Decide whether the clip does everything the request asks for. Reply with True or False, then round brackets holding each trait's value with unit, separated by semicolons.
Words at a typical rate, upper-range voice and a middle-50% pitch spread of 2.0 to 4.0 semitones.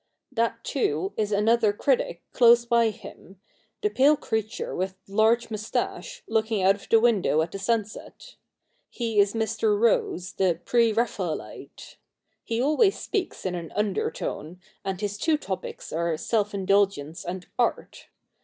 True (145 wpm; 215 Hz; 3.7 semitones)